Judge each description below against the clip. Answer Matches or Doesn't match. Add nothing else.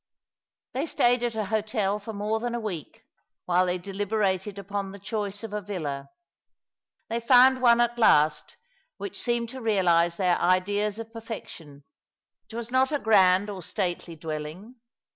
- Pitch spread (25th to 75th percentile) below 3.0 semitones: Doesn't match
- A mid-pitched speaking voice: Doesn't match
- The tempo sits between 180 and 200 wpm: Doesn't match